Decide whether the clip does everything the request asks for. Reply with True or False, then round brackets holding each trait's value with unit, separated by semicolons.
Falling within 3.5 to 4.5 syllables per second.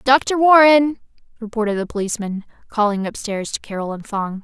False (5.4 syllables/s)